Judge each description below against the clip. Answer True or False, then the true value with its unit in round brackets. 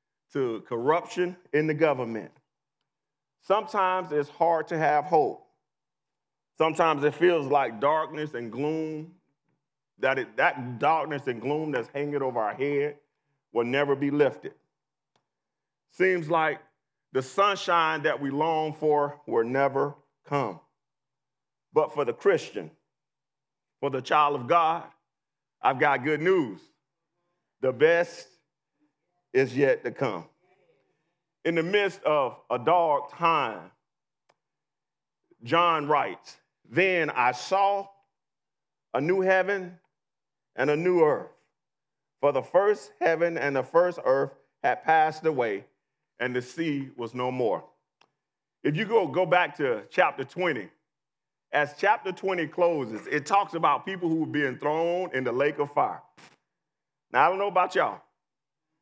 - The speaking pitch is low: False (155 Hz)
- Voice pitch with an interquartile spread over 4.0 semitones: False (3.7 semitones)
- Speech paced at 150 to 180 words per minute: False (135 wpm)